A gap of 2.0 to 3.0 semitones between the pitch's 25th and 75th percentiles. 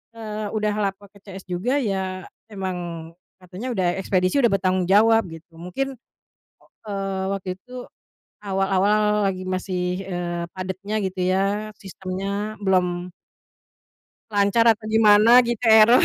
Yes: narrow, 2.5 semitones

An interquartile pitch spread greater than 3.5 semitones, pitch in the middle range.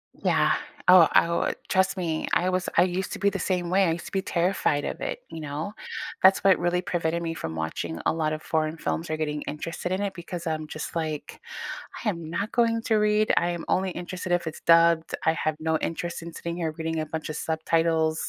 No: narrow, 2.6 semitones; medium, 170 Hz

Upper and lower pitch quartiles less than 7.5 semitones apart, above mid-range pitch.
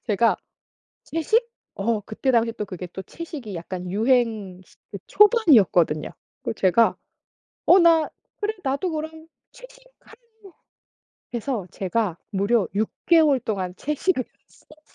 No: wide, 8.2 semitones; high, 235 Hz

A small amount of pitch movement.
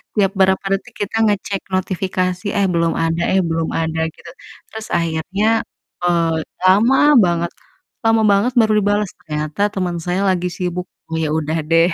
No: average, 3.4 semitones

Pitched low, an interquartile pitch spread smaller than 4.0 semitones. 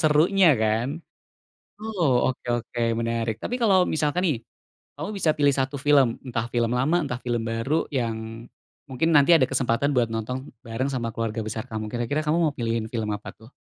No: low, 125 Hz; average, 4.4 semitones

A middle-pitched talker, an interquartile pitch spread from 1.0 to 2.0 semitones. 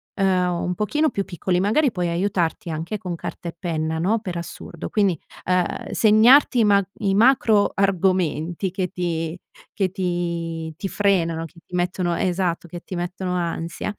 No: medium, 180 Hz; average, 2.7 semitones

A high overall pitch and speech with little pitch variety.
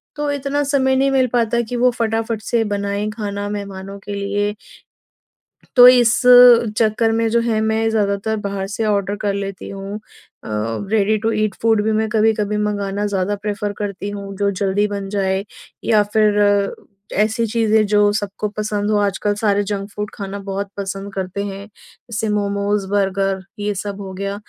Yes: high, 205 Hz; narrow, 1.7 semitones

